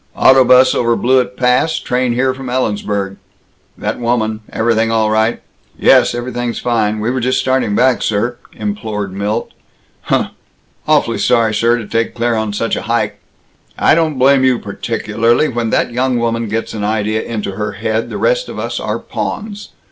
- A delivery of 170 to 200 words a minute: Yes, average, 175 wpm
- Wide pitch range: No, average, 2.7 semitones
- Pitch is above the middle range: No, low, 115 Hz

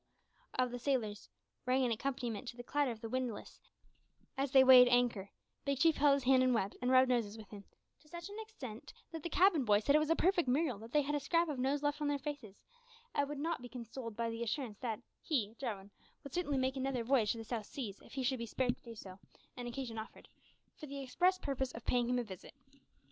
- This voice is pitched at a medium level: No, very high, 255 Hz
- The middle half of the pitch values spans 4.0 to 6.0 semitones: No, average, 3.6 semitones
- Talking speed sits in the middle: No, fast, 240 wpm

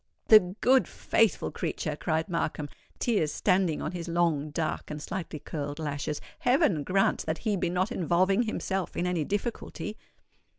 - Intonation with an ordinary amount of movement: Yes, average, 4.4 semitones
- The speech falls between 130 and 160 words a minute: Yes, average, 155 wpm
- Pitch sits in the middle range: Yes, medium, 175 Hz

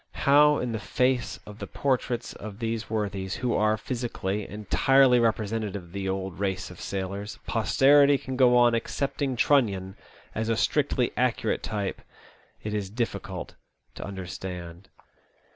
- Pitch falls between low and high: No, low, 110 Hz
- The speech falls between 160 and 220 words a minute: No, average, 145 wpm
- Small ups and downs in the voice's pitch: No, average, 4.3 semitones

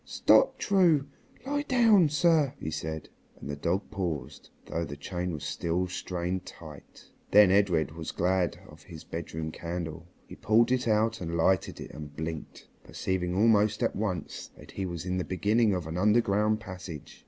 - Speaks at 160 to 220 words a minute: Yes, average, 170 wpm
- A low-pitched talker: Yes, very low, 90 Hz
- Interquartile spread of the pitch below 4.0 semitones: No, average, 4.7 semitones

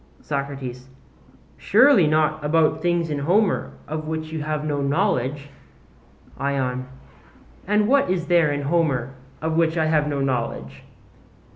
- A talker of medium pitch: Yes, medium, 155 Hz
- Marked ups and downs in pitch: No, average, 3.2 semitones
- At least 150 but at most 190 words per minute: No, slow, 135 wpm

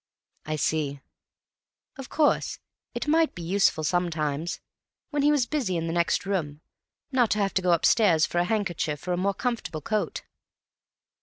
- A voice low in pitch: No, medium, 180 Hz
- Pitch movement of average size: No, wide, 5.9 semitones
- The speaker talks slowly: No, average, 165 wpm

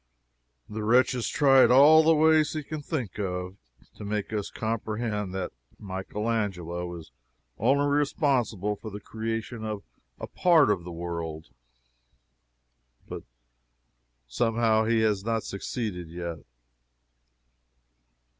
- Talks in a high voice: No, low, 110 Hz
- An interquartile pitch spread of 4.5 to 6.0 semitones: Yes, average, 4.8 semitones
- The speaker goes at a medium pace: No, slow, 120 wpm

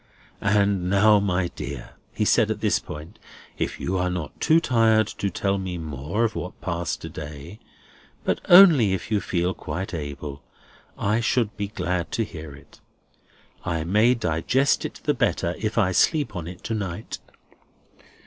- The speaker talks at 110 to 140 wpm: No, average, 160 wpm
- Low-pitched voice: Yes, very low, 95 Hz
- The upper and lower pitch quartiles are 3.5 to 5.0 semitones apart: Yes, average, 4.2 semitones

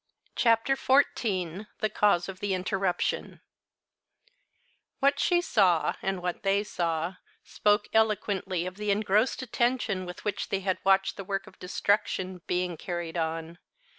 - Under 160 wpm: Yes, slow, 135 wpm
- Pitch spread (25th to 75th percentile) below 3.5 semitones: Yes, average, 2.9 semitones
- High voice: Yes, high, 195 Hz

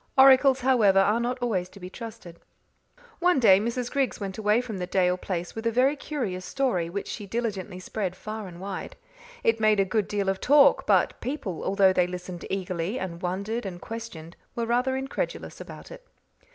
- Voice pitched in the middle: No, high, 210 Hz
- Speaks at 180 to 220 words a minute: Yes, average, 190 wpm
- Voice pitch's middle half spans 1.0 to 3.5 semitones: No, average, 4.7 semitones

